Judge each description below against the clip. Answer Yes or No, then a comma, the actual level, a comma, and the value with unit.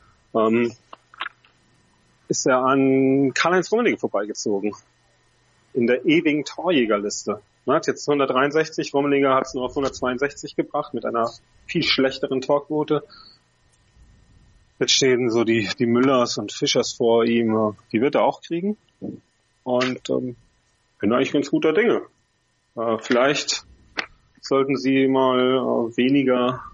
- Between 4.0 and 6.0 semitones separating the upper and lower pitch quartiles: No, average, 3.0 semitones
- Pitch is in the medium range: No, low, 130 Hz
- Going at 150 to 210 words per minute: No, average, 130 wpm